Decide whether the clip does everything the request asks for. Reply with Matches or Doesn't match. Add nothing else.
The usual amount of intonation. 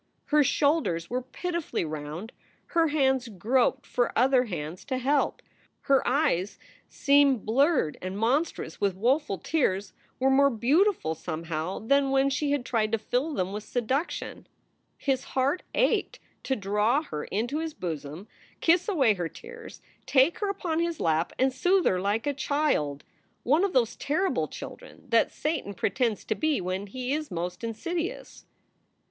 Doesn't match